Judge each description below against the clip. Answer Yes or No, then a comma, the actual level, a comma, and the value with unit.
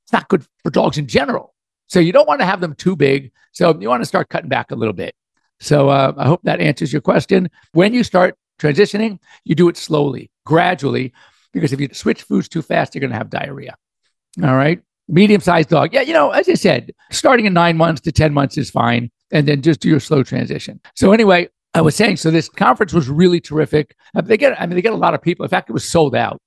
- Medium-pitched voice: Yes, medium, 165 Hz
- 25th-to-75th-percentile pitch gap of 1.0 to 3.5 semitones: No, average, 4.1 semitones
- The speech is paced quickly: Yes, fast, 250 wpm